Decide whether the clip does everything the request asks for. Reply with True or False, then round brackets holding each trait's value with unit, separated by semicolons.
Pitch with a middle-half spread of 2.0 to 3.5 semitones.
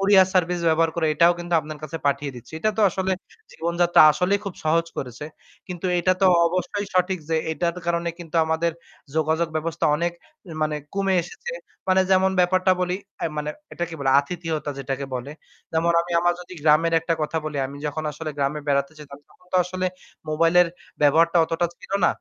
True (2.8 semitones)